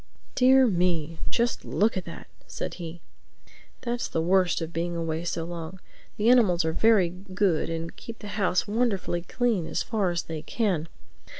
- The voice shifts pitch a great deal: No, average, 4.8 semitones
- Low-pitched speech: No, medium, 180 Hz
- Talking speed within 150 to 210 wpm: Yes, average, 170 wpm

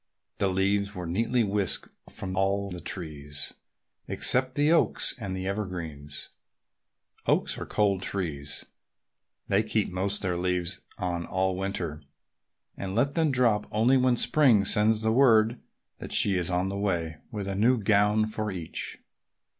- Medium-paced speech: Yes, average, 150 wpm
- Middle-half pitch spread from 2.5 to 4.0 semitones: Yes, average, 3.2 semitones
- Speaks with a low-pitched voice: Yes, low, 100 Hz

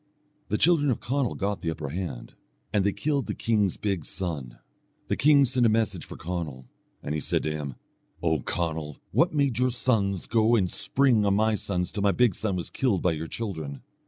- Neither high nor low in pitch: No, low, 100 Hz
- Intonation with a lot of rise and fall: Yes, wide, 6.4 semitones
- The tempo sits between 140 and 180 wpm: No, fast, 205 wpm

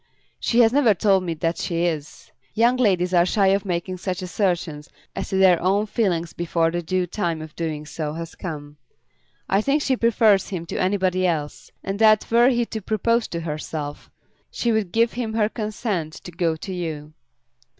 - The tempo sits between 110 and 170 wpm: No, average, 190 wpm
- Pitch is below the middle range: No, medium, 185 Hz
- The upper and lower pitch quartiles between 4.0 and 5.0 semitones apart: Yes, average, 4.5 semitones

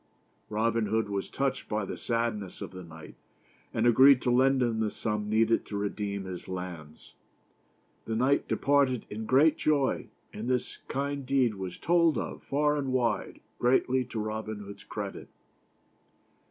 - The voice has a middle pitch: No, low, 115 Hz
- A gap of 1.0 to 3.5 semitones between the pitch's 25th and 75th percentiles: No, average, 4.2 semitones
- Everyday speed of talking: Yes, average, 155 wpm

